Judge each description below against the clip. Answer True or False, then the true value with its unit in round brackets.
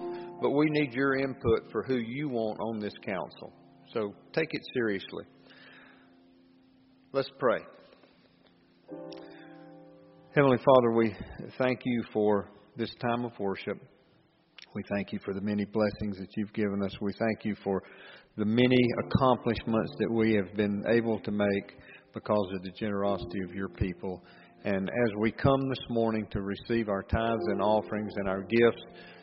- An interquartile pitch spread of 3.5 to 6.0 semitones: False (3.0 semitones)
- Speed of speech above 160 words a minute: False (155 wpm)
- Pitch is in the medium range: False (105 Hz)